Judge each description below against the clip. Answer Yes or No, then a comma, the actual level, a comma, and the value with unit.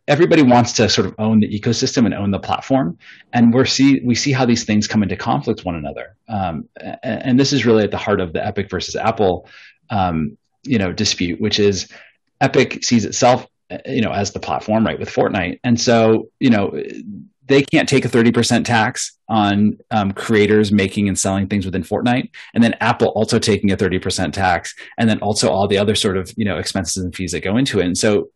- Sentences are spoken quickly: Yes, fast, 220 wpm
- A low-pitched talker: Yes, low, 110 Hz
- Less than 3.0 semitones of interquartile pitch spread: No, average, 3.3 semitones